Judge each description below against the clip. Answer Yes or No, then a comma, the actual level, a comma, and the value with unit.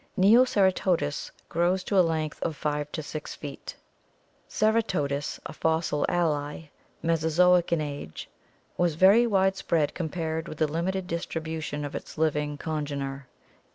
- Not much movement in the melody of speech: No, average, 3.4 semitones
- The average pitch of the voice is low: No, medium, 160 Hz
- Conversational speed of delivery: No, slow, 130 wpm